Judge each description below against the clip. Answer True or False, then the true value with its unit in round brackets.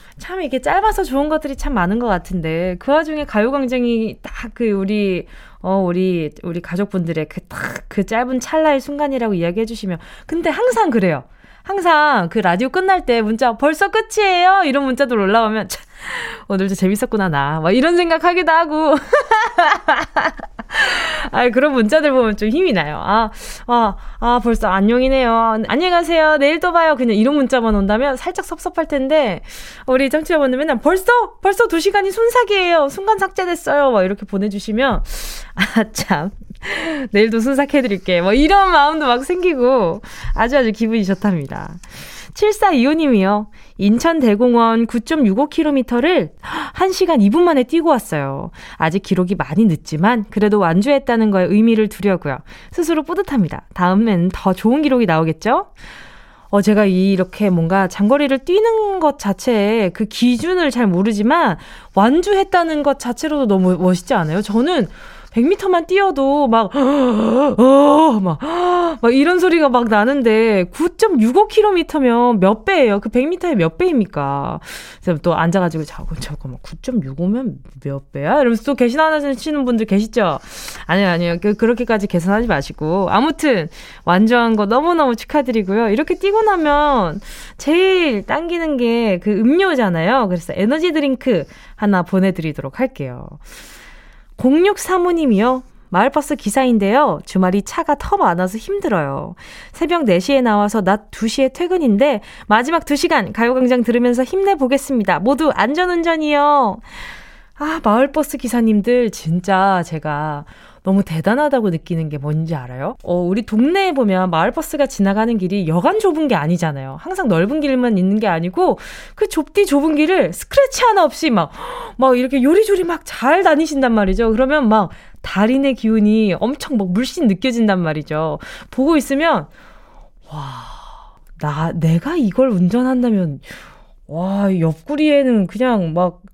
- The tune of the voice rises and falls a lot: True (7.4 semitones)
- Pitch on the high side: True (240 Hz)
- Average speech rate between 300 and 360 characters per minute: True (320 characters per minute)